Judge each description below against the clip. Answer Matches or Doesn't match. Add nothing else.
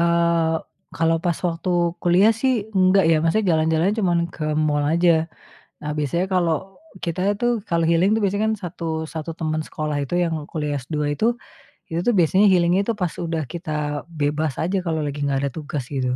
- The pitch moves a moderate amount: Matches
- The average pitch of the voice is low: Doesn't match